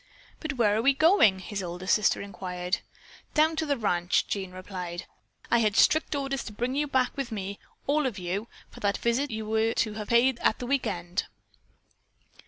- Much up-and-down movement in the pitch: Yes, wide, 5.9 semitones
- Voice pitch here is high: Yes, high, 220 Hz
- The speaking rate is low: No, average, 190 wpm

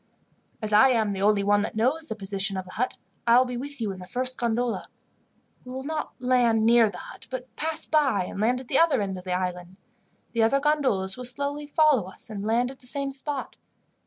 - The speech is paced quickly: Yes, fast, 230 wpm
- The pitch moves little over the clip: No, average, 4.7 semitones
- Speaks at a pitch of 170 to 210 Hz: No, high, 240 Hz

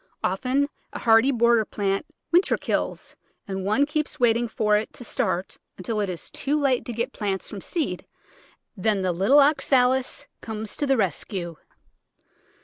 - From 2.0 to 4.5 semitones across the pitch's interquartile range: No, average, 5.1 semitones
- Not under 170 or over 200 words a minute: No, average, 155 wpm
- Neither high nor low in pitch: No, high, 225 Hz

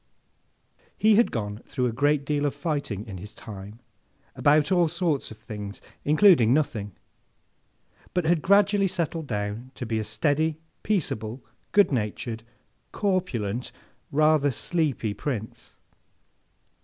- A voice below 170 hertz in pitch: Yes, medium, 140 Hz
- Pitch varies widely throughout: Yes, wide, 6.8 semitones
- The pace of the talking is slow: Yes, slow, 125 wpm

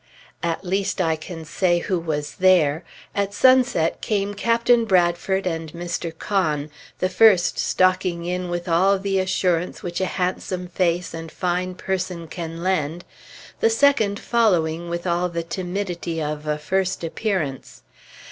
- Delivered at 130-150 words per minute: Yes, average, 145 wpm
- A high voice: No, medium, 180 Hz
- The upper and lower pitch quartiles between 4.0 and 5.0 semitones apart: No, narrow, 2.5 semitones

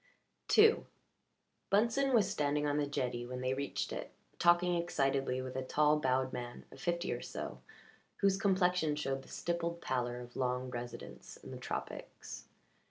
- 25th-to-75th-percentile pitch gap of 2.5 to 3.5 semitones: No, average, 5.2 semitones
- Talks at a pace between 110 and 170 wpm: Yes, average, 160 wpm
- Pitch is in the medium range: Yes, medium, 145 Hz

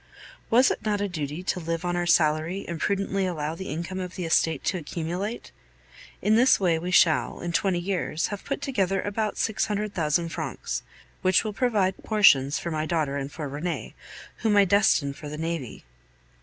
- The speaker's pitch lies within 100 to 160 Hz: No, medium, 175 Hz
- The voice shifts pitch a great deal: No, average, 3.9 semitones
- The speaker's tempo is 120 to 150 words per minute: No, average, 190 wpm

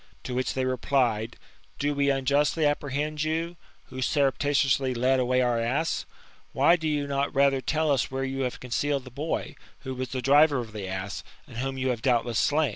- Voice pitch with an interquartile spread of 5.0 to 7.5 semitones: No, narrow, 2.4 semitones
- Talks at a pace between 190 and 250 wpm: Yes, average, 195 wpm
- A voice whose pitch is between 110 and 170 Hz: Yes, low, 135 Hz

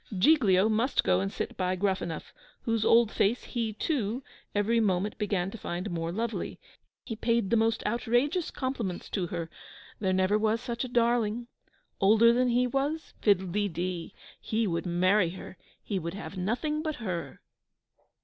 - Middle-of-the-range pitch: No, high, 215 Hz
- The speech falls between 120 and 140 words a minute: No, average, 165 wpm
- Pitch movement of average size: Yes, average, 4.1 semitones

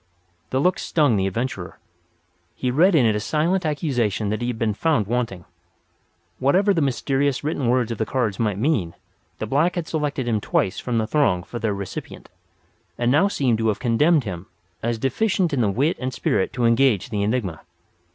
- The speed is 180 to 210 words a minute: Yes, average, 190 wpm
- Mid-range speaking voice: No, low, 125 Hz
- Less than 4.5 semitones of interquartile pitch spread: No, average, 5.3 semitones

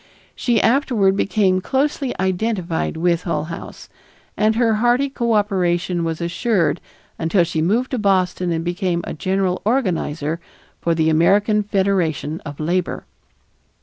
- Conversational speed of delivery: No, slow, 130 wpm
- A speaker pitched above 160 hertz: Yes, medium, 185 Hz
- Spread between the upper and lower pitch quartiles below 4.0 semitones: No, average, 4.3 semitones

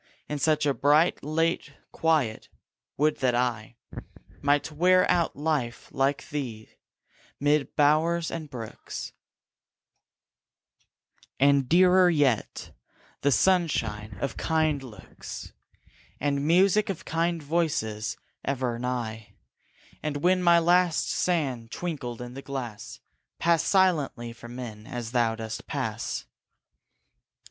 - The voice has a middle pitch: Yes, medium, 145 Hz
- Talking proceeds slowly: Yes, slow, 110 wpm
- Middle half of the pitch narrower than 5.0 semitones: No, average, 5.3 semitones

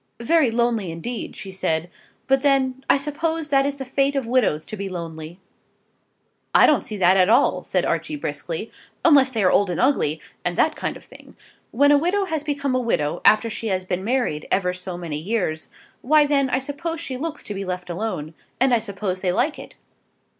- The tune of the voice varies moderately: No, wide, 7.3 semitones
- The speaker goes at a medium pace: No, fast, 210 wpm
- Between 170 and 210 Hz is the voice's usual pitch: No, high, 235 Hz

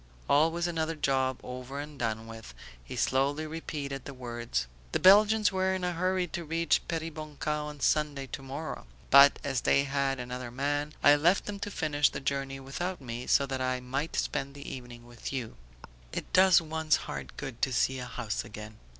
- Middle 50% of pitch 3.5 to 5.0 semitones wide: Yes, average, 3.9 semitones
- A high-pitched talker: No, medium, 140 Hz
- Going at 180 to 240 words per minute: Yes, average, 185 wpm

